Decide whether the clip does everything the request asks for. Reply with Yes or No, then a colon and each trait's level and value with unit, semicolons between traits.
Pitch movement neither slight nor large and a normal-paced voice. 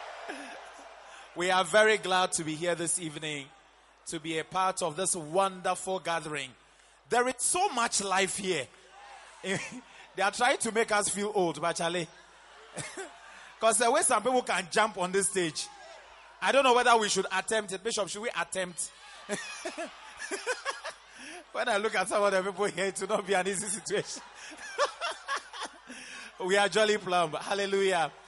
Yes: average, 3.7 semitones; average, 160 wpm